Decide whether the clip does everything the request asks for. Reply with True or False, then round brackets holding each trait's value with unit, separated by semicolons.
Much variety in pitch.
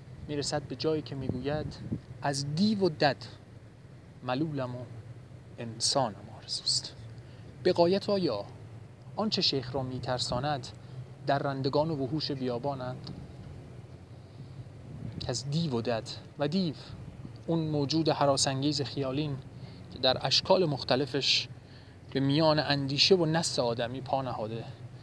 False (2.8 semitones)